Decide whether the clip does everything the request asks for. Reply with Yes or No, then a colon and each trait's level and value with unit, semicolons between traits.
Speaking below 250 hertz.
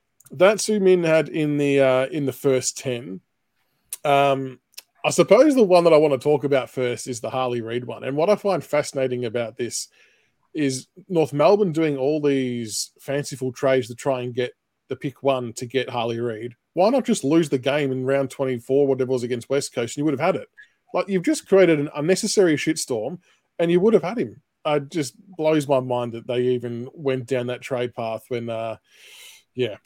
Yes: low, 135 Hz